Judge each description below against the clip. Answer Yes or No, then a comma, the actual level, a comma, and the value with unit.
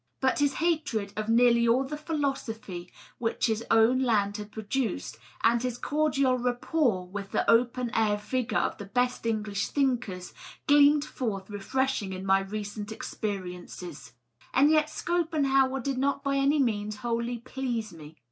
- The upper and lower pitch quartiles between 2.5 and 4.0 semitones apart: No, average, 4.6 semitones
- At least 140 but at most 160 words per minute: Yes, average, 150 wpm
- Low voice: No, high, 235 Hz